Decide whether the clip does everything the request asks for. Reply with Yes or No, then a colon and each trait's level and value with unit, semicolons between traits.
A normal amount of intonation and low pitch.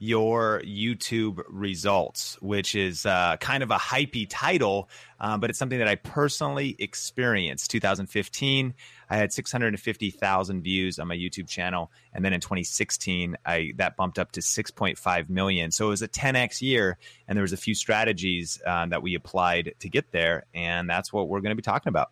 Yes: average, 3.6 semitones; low, 100 Hz